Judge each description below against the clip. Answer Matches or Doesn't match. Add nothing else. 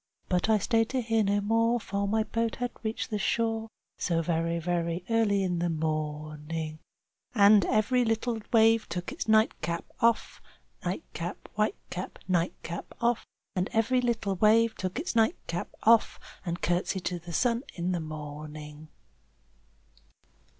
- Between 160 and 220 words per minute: Doesn't match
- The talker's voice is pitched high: Matches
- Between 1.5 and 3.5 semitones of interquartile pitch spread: Doesn't match